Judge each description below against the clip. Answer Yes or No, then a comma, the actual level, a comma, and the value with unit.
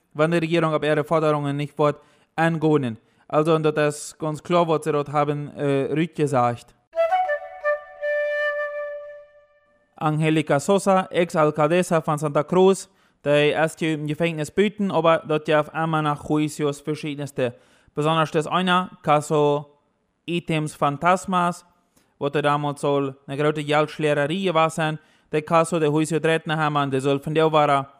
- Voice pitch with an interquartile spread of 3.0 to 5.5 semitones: No, narrow, 2.5 semitones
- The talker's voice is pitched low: No, medium, 155 Hz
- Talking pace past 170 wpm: No, average, 130 wpm